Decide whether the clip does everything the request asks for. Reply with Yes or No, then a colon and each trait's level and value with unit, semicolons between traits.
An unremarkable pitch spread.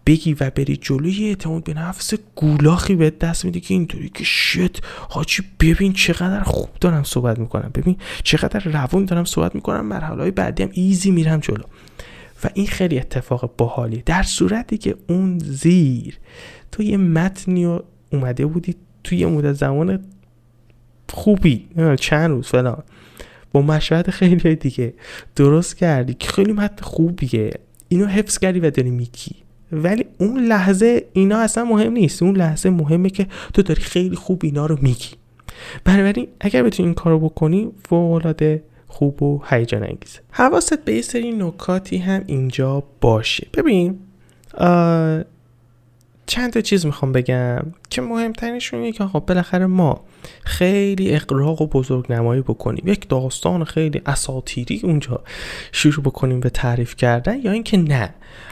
No: wide, 5.7 semitones